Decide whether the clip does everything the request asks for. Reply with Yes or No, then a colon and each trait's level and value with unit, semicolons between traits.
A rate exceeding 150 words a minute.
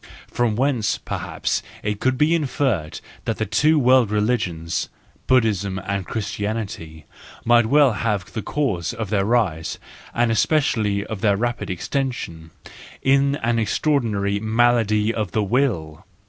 No: slow, 135 wpm